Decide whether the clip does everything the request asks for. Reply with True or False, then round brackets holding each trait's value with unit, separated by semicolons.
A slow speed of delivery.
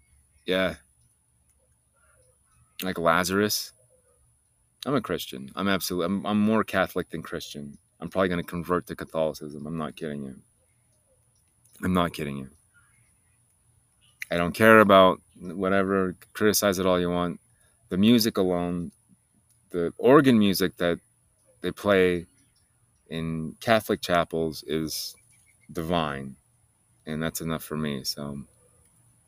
True (120 wpm)